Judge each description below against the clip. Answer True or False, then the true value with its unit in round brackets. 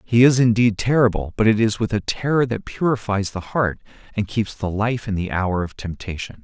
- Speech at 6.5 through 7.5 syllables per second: False (5.2 syllables/s)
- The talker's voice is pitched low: True (110 Hz)